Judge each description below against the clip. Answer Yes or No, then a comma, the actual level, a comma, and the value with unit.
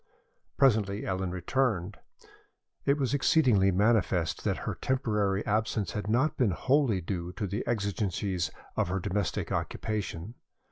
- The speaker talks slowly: Yes, slow, 130 wpm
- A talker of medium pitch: No, low, 105 Hz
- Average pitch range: Yes, average, 3.9 semitones